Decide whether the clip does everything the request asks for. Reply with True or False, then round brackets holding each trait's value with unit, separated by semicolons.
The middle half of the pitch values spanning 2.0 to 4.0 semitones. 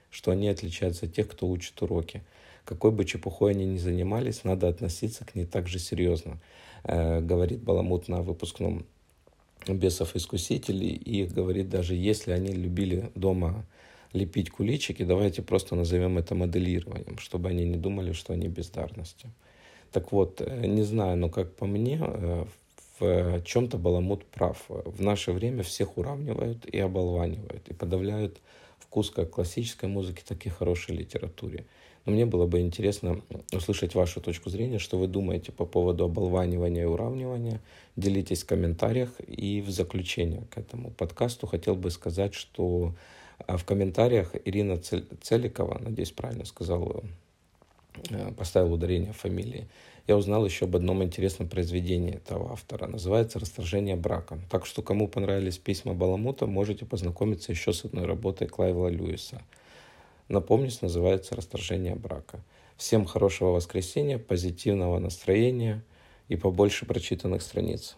True (3.3 semitones)